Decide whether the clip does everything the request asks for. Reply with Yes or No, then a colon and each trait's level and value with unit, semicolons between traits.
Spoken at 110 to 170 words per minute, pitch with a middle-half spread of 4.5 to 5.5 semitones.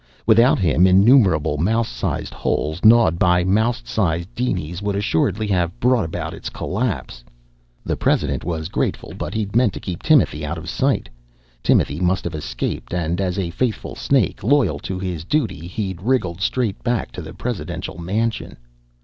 Yes: average, 165 wpm; average, 4.9 semitones